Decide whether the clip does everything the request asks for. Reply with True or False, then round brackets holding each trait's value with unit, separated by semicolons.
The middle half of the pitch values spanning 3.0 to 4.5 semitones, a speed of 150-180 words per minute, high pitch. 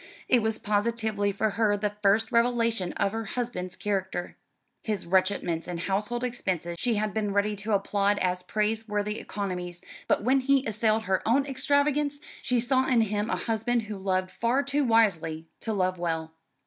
True (3.4 semitones; 170 wpm; 210 Hz)